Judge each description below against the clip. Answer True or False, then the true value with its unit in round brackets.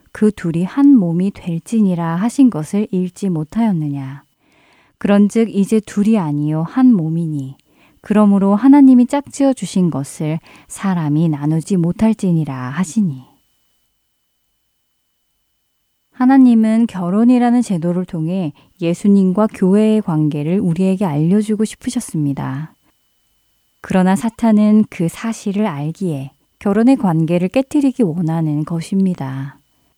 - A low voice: False (190 Hz)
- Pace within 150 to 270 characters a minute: True (265 characters per minute)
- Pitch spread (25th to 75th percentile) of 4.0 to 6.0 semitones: True (5.4 semitones)